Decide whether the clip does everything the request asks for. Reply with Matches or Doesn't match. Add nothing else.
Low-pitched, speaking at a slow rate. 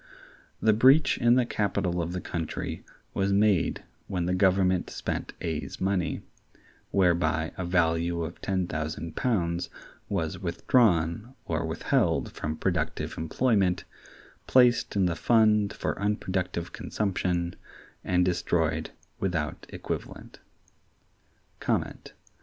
Matches